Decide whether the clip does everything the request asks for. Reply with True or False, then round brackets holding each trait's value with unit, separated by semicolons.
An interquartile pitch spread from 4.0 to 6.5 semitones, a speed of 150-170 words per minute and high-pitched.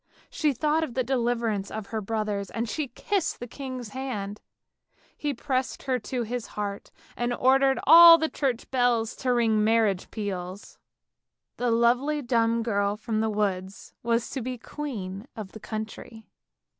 False (3.5 semitones; 155 wpm; 235 Hz)